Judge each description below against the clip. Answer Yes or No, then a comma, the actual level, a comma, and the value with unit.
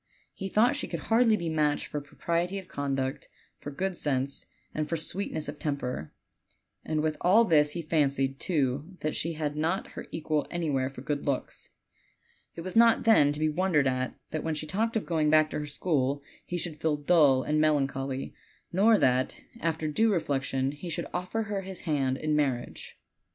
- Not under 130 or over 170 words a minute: No, average, 190 wpm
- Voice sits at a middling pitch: Yes, medium, 155 Hz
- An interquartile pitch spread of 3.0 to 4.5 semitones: Yes, average, 3.8 semitones